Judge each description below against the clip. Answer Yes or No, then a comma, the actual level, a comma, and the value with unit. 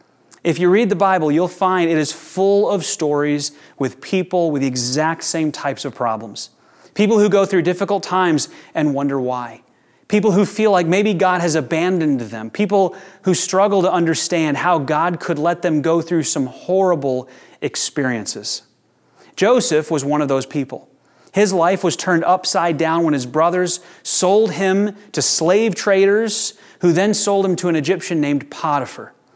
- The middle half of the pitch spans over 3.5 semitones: Yes, average, 4.0 semitones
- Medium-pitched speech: Yes, medium, 175 Hz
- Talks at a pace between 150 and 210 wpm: Yes, average, 170 wpm